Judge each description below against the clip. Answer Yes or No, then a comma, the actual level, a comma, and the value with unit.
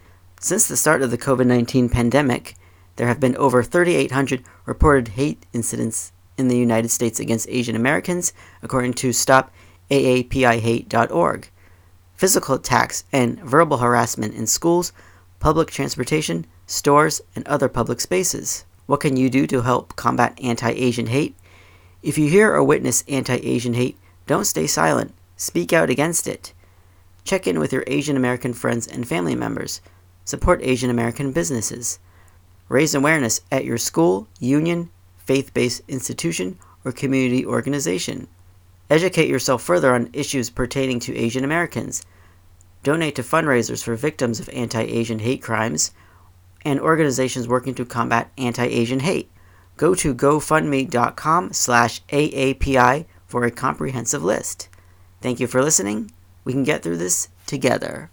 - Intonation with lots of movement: Yes, wide, 6.5 semitones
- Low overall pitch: Yes, low, 120 Hz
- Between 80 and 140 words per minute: Yes, slow, 135 wpm